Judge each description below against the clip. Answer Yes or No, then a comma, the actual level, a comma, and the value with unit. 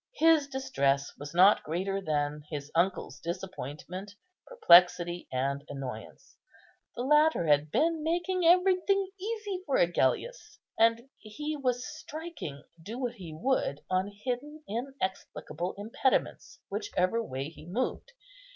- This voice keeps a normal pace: No, slow, 120 wpm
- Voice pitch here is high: Yes, high, 210 Hz